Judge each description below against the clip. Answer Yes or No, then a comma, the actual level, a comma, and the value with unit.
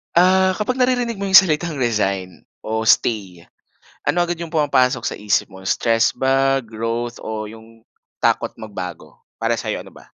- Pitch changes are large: Yes, wide, 7.8 semitones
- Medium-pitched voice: No, low, 120 Hz